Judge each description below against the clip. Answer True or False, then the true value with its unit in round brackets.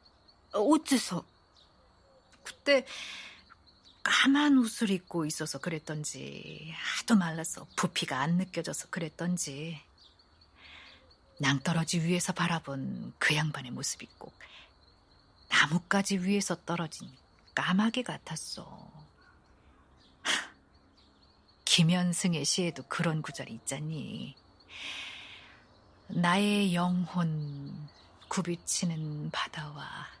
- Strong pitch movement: False (4.8 semitones)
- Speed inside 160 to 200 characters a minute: True (190 characters per minute)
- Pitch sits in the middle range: True (165 Hz)